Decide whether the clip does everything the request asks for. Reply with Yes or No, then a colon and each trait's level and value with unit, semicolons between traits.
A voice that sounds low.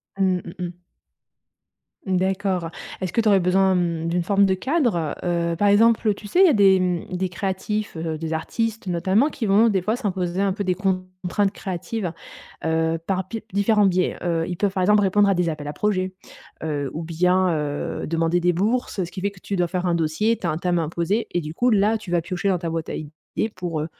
No: medium, 185 Hz